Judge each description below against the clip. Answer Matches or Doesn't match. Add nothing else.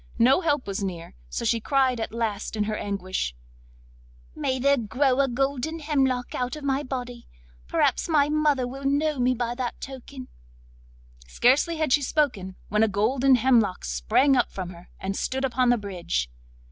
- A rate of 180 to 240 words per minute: Doesn't match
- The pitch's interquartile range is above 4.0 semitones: Matches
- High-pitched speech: Matches